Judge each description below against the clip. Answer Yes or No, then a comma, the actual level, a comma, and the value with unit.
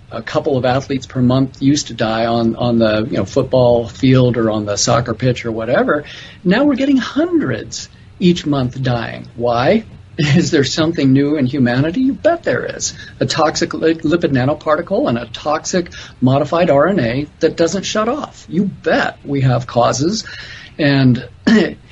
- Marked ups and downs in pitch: Yes, wide, 5.8 semitones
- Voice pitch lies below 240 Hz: Yes, low, 135 Hz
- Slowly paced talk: No, average, 165 wpm